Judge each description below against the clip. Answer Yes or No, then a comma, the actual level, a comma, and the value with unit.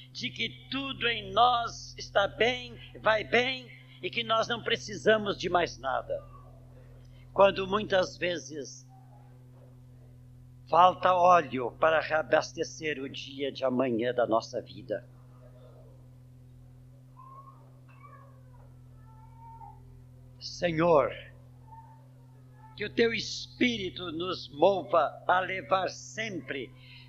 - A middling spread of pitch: Yes, average, 4.2 semitones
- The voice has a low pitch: Yes, low, 130 Hz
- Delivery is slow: Yes, slow, 90 wpm